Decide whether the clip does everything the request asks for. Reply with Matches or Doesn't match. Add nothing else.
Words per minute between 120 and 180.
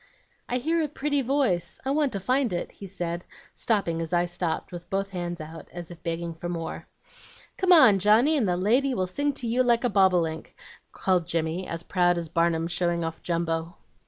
Doesn't match